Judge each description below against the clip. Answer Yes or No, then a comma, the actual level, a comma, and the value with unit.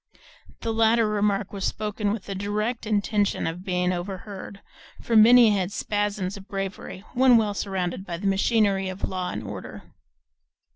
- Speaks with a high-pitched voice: Yes, high, 200 Hz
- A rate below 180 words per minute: Yes, average, 155 wpm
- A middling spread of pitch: No, narrow, 2.1 semitones